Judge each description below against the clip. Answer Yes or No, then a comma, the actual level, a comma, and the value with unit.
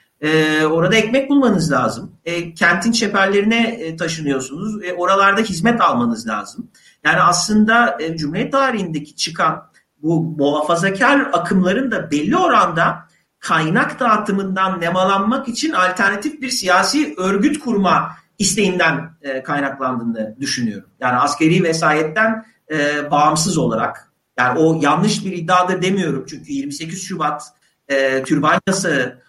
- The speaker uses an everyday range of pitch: No, wide, 6.0 semitones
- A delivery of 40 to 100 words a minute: No, average, 115 wpm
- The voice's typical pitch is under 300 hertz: Yes, medium, 185 Hz